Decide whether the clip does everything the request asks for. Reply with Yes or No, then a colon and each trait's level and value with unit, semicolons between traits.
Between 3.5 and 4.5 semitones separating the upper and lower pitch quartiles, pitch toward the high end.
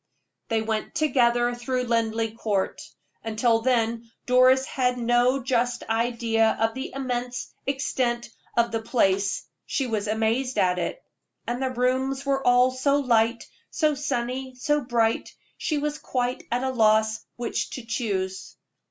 No: narrow, 2.4 semitones; high, 240 Hz